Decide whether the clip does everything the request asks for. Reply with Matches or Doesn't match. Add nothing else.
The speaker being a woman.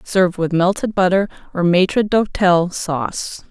Matches